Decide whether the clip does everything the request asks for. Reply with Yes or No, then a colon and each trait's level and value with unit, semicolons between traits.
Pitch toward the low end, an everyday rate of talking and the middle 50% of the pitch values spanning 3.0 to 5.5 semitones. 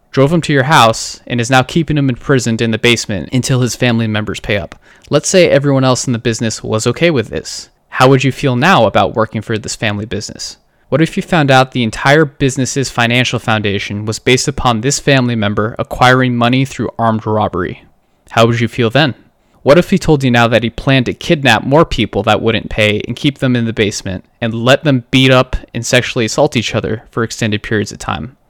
No: low, 120 Hz; fast, 220 wpm; average, 3.3 semitones